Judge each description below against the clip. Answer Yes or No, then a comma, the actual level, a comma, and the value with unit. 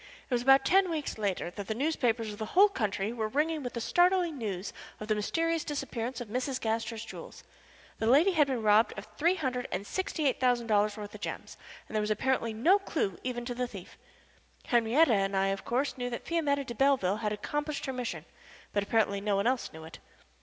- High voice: Yes, high, 240 Hz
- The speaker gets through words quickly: Yes, fast, 215 wpm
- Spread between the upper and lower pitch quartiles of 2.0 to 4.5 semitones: No, average, 4.9 semitones